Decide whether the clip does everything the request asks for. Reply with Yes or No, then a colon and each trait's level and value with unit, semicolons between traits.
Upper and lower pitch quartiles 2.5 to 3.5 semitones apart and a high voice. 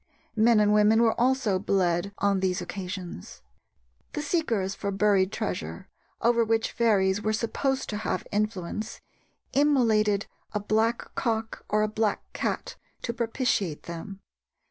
Yes: average, 2.8 semitones; high, 215 Hz